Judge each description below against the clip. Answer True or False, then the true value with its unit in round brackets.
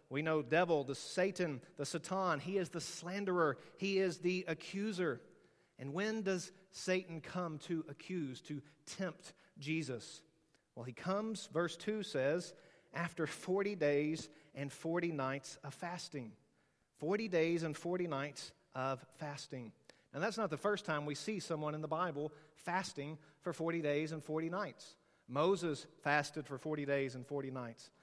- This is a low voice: False (160 Hz)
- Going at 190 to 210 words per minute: False (155 wpm)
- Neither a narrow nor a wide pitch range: True (3.9 semitones)